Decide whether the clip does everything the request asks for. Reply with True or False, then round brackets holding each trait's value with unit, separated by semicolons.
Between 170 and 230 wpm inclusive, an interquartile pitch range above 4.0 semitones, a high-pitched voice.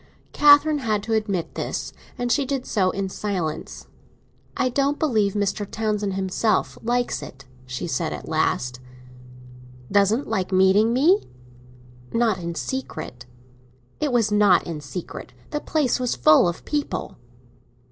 False (135 wpm; 5.3 semitones; 210 Hz)